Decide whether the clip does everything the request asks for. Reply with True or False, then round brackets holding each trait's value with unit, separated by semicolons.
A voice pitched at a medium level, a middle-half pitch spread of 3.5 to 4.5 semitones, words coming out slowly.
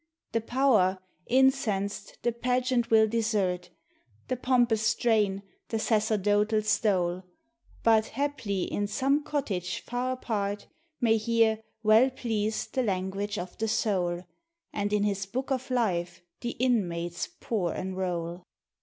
False (215 Hz; 3.8 semitones; 125 wpm)